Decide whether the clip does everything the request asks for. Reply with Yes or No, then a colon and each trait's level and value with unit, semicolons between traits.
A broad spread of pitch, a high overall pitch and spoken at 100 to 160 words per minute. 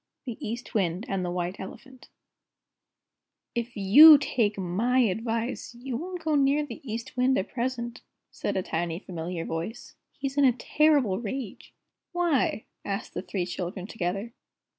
Yes: wide, 5.8 semitones; high, 230 Hz; average, 150 wpm